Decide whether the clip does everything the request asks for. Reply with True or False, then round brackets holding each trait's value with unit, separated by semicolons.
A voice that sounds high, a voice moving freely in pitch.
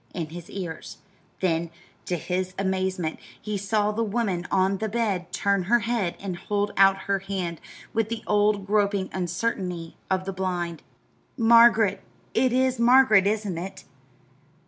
False (195 Hz; 2.8 semitones)